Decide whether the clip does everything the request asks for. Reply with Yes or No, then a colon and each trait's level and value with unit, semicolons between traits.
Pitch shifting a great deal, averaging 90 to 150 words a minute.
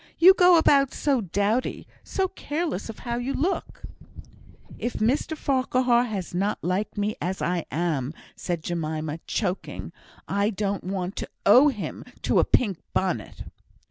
Yes: wide, 6.3 semitones; average, 145 wpm